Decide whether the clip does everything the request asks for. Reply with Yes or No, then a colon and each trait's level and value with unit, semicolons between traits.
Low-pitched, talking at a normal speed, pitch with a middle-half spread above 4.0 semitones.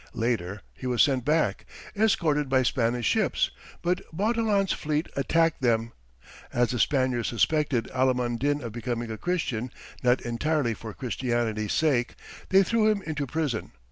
Yes: low, 130 Hz; average, 145 wpm; average, 5.0 semitones